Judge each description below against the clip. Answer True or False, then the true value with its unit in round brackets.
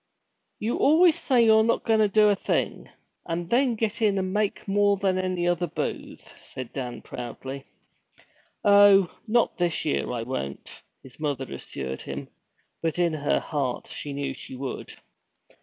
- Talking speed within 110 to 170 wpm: True (160 wpm)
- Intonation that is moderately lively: False (7.3 semitones)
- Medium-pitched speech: True (180 Hz)